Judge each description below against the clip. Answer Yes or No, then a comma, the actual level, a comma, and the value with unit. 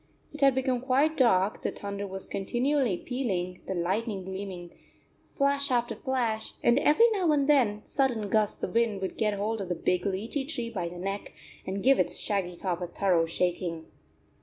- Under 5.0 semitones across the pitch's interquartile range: No, wide, 5.6 semitones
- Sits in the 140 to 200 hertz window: No, high, 210 Hz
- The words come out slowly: No, average, 185 wpm